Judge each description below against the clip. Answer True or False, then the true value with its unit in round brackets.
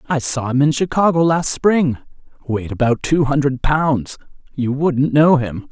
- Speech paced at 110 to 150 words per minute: True (145 wpm)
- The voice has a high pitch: False (145 Hz)